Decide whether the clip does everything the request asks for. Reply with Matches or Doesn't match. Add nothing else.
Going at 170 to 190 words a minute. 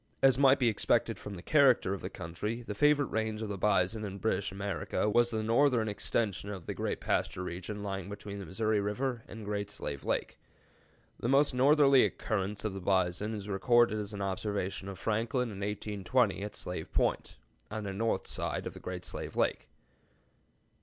Matches